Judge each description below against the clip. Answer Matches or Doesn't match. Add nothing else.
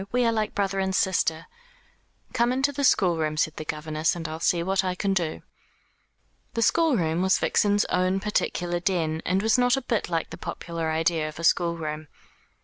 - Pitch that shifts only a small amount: Doesn't match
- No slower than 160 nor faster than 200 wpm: Matches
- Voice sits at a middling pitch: Matches